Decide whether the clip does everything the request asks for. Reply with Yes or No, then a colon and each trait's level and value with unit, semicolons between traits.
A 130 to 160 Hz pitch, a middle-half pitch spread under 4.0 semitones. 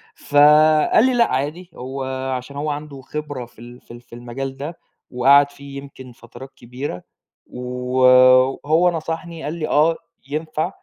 Yes: medium, 140 Hz; average, 3.5 semitones